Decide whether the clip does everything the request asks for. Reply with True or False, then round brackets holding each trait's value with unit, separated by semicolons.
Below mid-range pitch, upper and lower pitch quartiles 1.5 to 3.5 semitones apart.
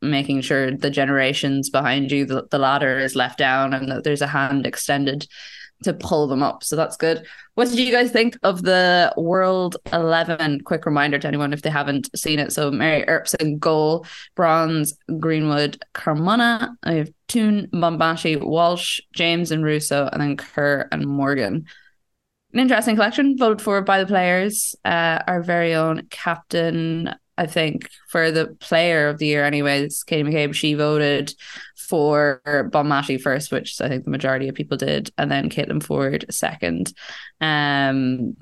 False (155 Hz; 3.2 semitones)